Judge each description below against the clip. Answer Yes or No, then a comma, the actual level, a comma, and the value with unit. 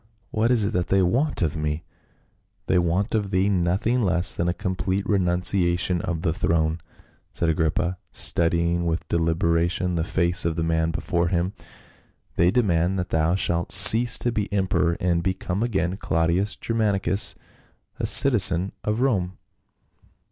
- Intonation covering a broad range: No, average, 2.7 semitones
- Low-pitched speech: Yes, very low, 90 Hz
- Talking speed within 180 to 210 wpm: No, average, 155 wpm